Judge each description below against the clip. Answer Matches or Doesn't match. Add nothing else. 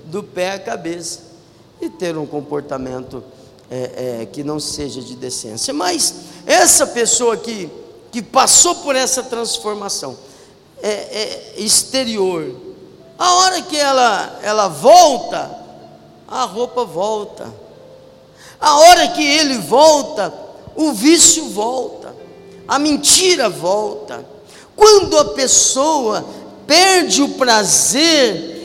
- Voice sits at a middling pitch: Doesn't match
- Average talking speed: Doesn't match